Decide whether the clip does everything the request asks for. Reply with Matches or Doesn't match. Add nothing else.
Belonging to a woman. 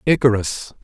Doesn't match